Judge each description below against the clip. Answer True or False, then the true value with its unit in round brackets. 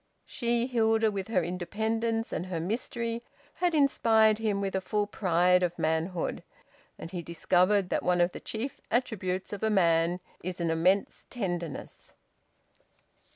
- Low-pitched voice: False (195 Hz)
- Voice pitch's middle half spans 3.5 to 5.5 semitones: True (4.1 semitones)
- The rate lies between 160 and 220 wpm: False (150 wpm)